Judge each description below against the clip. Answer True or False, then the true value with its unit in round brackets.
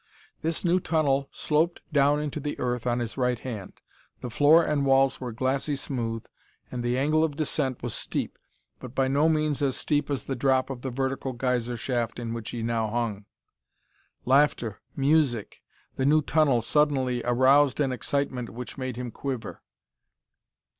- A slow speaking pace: False (165 wpm)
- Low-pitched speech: True (130 Hz)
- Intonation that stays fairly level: False (3.1 semitones)